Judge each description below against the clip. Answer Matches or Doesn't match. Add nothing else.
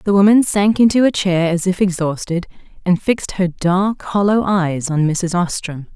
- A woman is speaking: Matches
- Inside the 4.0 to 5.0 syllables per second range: Matches